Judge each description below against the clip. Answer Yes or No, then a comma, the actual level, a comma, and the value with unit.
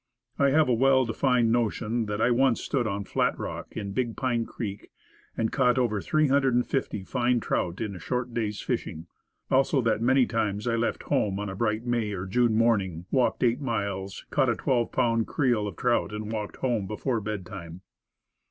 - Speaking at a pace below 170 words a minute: No, average, 185 wpm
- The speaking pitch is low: Yes, low, 115 Hz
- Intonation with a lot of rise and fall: No, average, 3.2 semitones